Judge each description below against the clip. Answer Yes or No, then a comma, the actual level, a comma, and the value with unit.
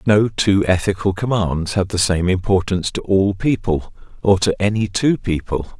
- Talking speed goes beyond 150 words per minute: Yes, average, 165 wpm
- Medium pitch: No, very low, 95 Hz